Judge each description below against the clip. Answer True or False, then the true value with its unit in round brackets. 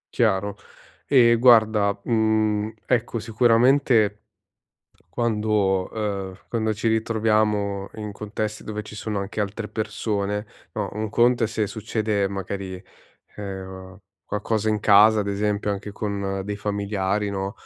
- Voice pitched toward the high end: False (105 Hz)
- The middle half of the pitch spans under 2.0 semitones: True (1.6 semitones)